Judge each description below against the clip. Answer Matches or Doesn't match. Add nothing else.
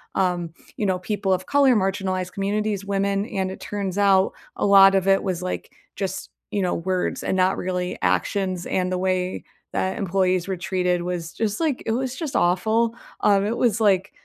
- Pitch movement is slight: Matches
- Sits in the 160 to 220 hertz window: Matches